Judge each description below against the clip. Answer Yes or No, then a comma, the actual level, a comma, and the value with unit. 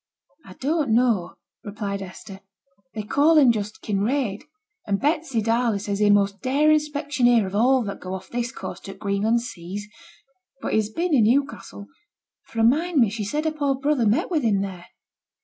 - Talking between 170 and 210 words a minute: Yes, average, 185 wpm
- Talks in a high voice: Yes, high, 230 Hz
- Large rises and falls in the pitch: Yes, wide, 5.7 semitones